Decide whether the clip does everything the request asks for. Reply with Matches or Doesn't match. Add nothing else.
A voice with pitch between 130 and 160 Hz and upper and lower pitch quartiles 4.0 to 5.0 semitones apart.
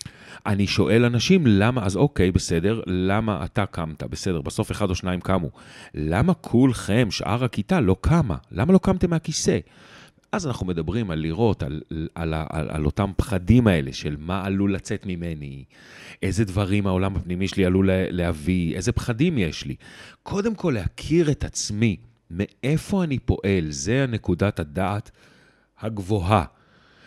Doesn't match